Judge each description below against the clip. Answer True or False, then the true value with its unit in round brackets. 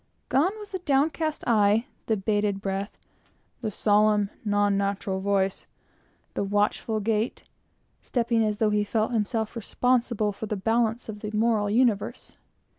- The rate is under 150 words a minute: True (135 wpm)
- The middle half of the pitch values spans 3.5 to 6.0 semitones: False (2.4 semitones)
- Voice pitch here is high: True (215 Hz)